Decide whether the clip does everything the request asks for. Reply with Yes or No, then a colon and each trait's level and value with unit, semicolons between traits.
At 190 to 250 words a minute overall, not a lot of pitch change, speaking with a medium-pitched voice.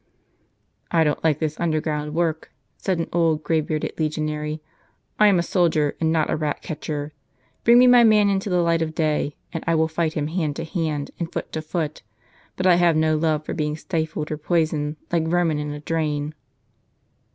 Yes: average, 195 wpm; narrow, 1.9 semitones; medium, 160 Hz